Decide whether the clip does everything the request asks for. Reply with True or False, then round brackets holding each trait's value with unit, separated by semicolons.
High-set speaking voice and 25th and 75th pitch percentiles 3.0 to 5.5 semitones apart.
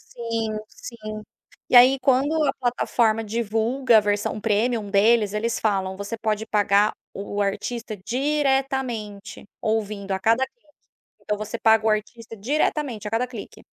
False (220 Hz; 2.6 semitones)